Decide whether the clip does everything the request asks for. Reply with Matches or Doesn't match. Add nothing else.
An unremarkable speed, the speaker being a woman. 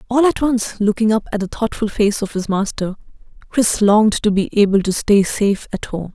Doesn't match